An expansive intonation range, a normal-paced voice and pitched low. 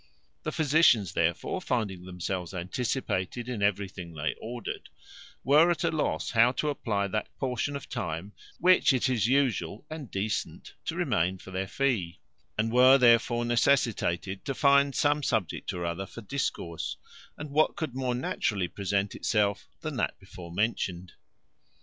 Yes: wide, 6.0 semitones; average, 150 wpm; low, 115 Hz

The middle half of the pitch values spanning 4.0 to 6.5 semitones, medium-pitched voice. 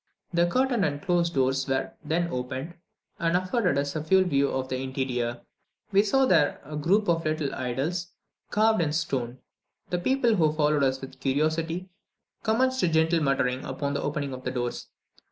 Yes: average, 4.9 semitones; medium, 155 Hz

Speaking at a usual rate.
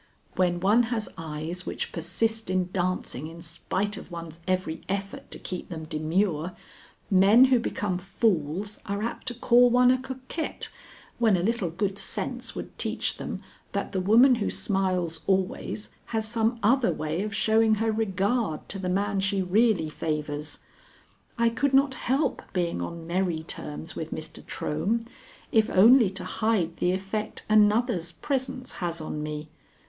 Yes: average, 160 wpm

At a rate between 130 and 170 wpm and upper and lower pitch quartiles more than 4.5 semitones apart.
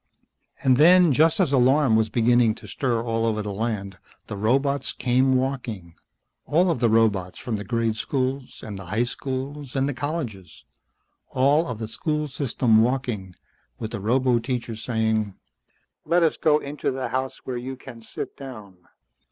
No: average, 165 wpm; average, 3.6 semitones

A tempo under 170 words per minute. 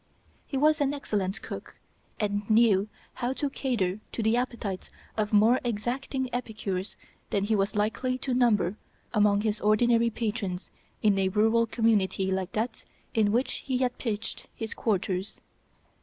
Yes: average, 150 wpm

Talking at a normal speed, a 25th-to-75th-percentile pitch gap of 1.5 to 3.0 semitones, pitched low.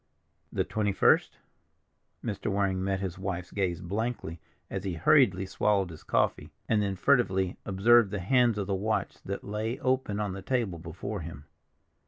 Yes: average, 165 wpm; narrow, 2.6 semitones; low, 100 Hz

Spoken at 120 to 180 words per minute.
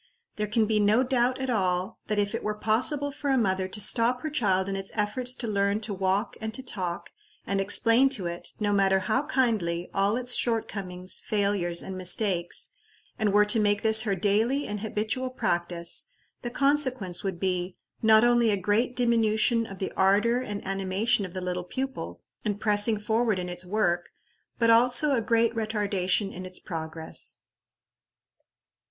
Yes: average, 175 wpm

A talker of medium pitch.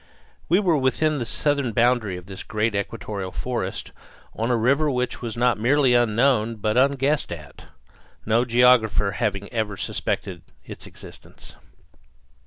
No: low, 120 Hz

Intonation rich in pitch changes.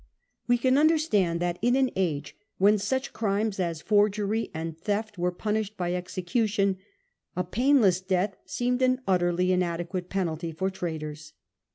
No: average, 3.8 semitones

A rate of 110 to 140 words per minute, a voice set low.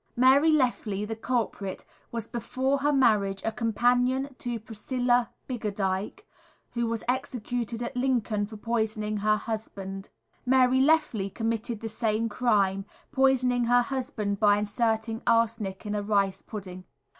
No: slow, 135 wpm; high, 230 Hz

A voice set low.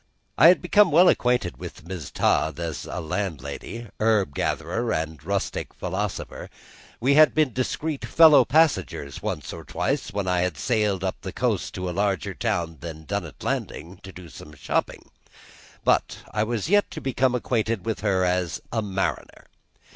Yes: low, 100 Hz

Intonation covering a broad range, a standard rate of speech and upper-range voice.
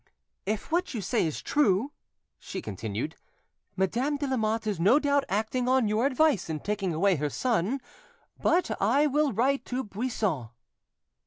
Yes: wide, 6.0 semitones; average, 155 wpm; high, 220 Hz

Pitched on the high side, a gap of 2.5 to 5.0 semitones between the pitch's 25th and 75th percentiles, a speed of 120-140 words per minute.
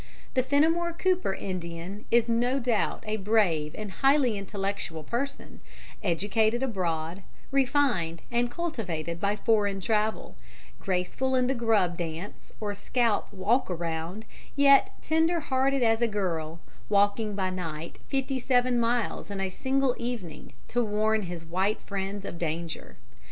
No: high, 210 Hz; wide, 5.4 semitones; slow, 135 wpm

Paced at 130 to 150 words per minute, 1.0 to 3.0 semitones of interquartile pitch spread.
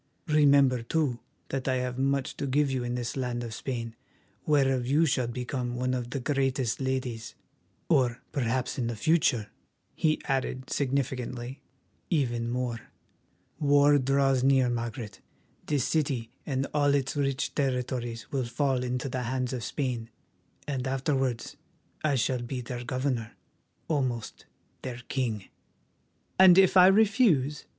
Yes: average, 140 wpm; narrow, 2.4 semitones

